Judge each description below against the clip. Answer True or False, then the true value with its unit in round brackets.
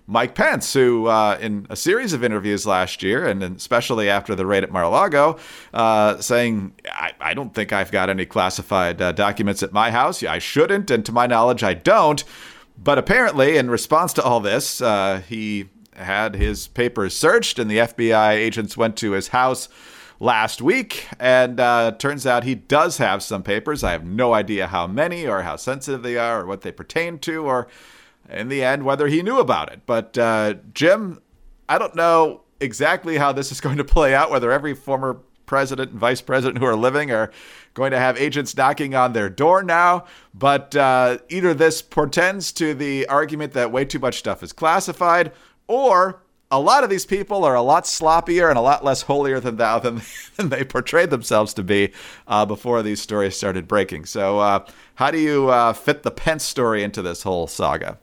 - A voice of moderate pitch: False (125 Hz)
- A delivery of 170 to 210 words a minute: True (200 wpm)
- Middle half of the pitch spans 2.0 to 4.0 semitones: False (5.5 semitones)